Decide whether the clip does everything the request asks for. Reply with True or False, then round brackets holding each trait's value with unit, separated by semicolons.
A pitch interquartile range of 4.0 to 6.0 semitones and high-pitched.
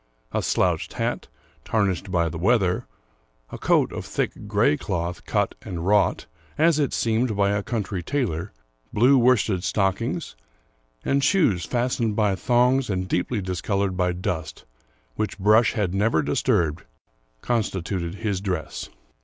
False (4.6 semitones; 100 Hz)